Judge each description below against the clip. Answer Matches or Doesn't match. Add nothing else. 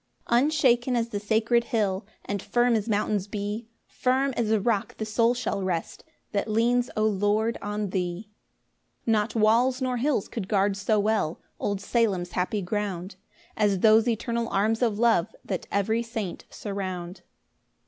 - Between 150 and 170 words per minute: Matches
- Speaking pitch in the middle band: Doesn't match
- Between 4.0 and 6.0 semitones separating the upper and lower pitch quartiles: Doesn't match